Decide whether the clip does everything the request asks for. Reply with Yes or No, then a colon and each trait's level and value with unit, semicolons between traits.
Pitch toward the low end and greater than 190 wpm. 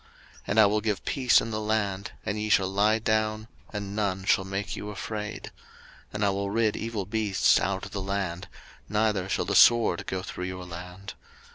Yes: low, 100 Hz; average, 200 wpm